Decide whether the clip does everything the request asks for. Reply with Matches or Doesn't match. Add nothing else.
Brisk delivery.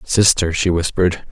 Doesn't match